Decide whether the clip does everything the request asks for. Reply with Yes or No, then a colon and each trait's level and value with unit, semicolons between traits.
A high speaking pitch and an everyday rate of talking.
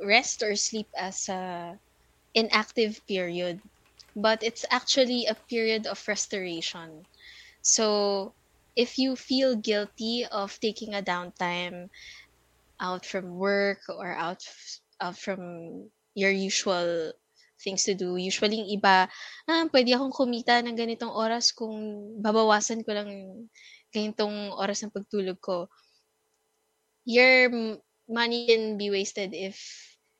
Yes: high, 210 Hz; average, 120 wpm